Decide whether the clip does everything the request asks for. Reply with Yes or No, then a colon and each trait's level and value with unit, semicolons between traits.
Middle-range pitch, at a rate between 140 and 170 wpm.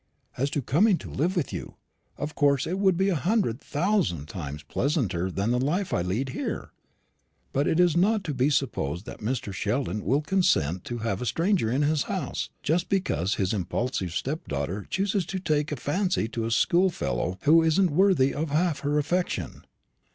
No: medium, 145 Hz; average, 185 wpm